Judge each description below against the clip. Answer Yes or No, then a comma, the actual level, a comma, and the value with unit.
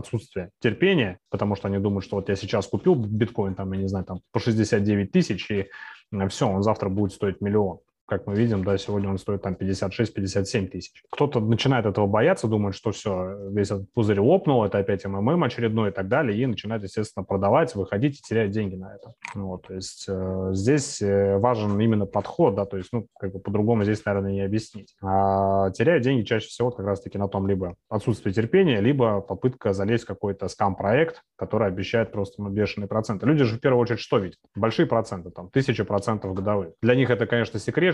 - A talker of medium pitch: No, low, 105 Hz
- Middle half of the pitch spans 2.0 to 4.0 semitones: Yes, average, 3.0 semitones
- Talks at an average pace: No, fast, 200 wpm